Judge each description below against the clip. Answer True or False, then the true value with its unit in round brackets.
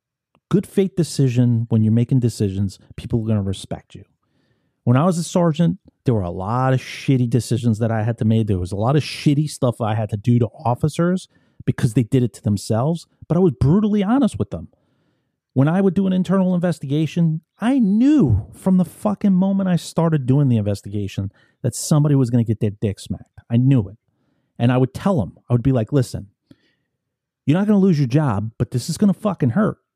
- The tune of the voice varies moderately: False (6.5 semitones)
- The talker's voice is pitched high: False (130 Hz)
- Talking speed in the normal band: False (220 wpm)